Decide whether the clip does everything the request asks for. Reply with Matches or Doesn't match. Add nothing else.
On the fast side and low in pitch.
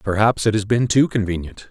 Matches